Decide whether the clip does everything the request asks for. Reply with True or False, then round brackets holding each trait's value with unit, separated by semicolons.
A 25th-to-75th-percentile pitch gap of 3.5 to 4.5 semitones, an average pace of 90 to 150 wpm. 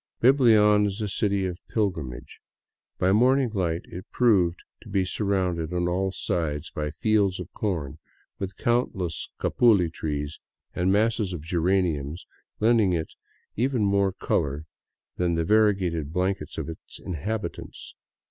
True (3.9 semitones; 140 wpm)